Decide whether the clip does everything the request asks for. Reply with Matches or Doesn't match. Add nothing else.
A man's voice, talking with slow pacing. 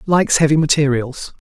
Matches